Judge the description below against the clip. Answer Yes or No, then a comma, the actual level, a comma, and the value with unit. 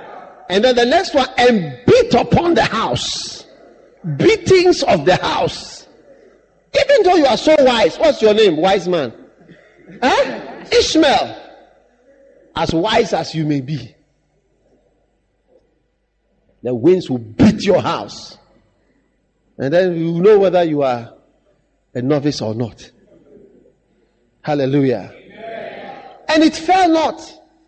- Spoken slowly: Yes, slow, 120 wpm